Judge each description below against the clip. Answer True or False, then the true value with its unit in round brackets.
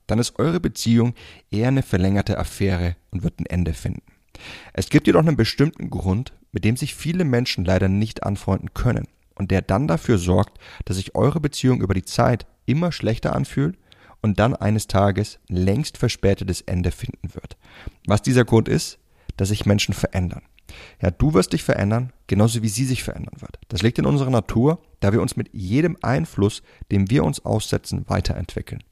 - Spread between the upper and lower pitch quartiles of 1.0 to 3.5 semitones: False (4.5 semitones)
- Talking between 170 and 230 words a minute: True (180 wpm)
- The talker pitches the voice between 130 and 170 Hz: False (105 Hz)